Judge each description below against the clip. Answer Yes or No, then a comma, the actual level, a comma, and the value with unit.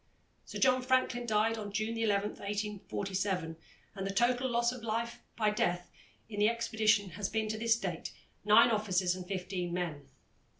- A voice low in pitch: No, high, 210 Hz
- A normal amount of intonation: Yes, average, 3.1 semitones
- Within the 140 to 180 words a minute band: Yes, average, 165 wpm